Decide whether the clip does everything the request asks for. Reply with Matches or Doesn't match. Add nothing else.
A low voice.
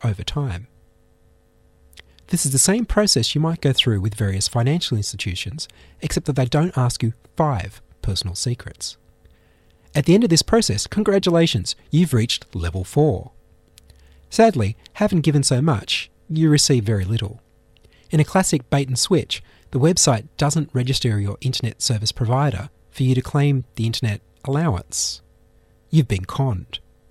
Matches